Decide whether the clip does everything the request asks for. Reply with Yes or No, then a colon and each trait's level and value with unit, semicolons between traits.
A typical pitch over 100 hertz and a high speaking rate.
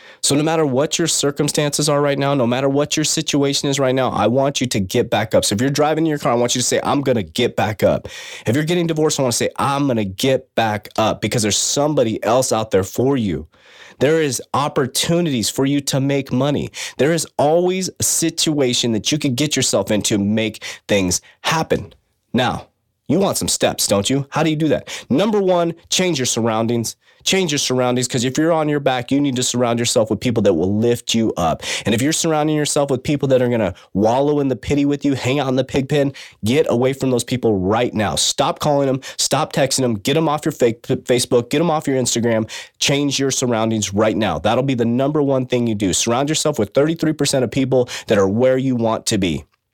Yes: low, 135 Hz; fast, 235 wpm